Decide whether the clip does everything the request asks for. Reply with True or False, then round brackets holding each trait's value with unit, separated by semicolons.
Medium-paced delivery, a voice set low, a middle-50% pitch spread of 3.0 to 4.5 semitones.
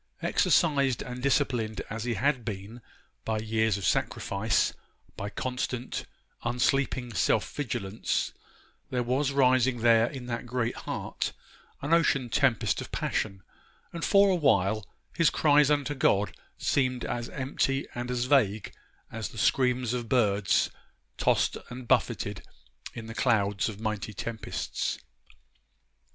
False (130 wpm; 120 Hz; 3.4 semitones)